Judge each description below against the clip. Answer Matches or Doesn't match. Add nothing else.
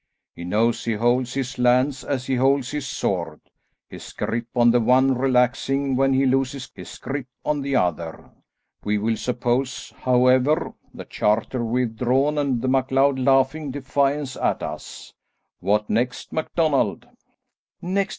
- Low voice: Matches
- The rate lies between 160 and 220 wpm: Doesn't match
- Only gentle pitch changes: Matches